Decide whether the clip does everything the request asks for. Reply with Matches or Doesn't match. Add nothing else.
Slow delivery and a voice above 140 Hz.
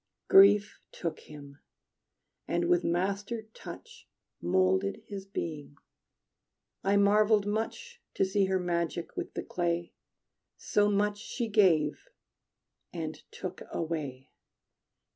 Matches